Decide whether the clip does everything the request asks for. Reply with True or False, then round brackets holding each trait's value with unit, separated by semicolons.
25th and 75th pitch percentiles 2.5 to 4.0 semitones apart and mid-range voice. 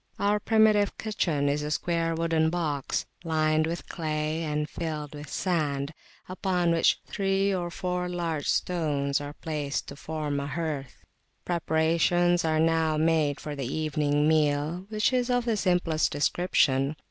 True (3.0 semitones; 160 Hz)